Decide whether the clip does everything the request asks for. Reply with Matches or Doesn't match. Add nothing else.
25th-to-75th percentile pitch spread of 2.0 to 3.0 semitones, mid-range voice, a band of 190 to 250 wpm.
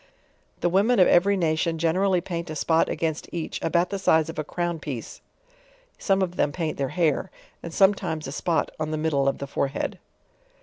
Matches